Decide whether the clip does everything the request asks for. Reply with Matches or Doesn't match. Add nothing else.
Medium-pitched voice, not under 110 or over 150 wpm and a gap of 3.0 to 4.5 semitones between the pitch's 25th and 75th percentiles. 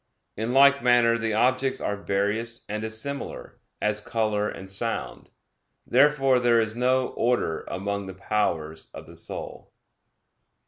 Doesn't match